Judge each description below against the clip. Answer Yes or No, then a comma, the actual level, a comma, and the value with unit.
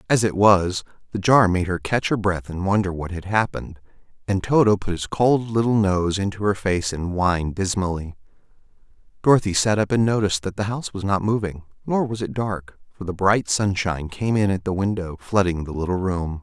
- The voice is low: Yes, low, 100 Hz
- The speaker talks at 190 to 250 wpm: Yes, fast, 205 wpm